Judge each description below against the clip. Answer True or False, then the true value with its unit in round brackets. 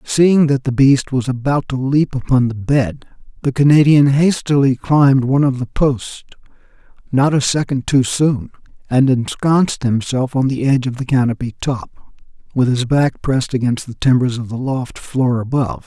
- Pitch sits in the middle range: False (130 Hz)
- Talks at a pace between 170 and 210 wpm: True (175 wpm)